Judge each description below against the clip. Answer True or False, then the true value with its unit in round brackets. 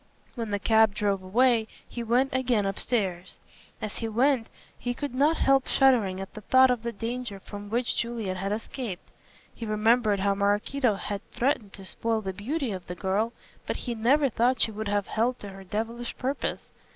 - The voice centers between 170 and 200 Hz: False (225 Hz)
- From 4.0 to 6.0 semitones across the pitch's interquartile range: False (3.6 semitones)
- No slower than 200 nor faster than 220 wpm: False (190 wpm)